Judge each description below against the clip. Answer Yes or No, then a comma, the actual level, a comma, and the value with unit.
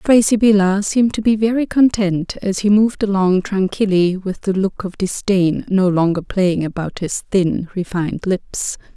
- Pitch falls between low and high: No, high, 195 Hz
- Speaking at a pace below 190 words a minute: Yes, average, 165 wpm